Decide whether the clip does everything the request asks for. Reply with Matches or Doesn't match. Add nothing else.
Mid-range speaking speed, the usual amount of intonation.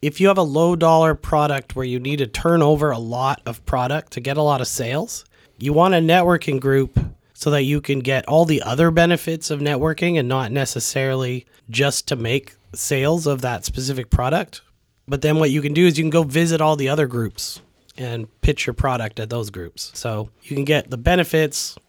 Doesn't match